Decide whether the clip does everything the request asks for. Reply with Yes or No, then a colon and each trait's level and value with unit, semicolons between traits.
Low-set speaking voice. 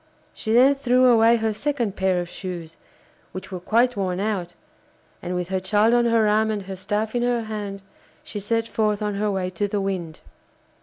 No: high, 210 Hz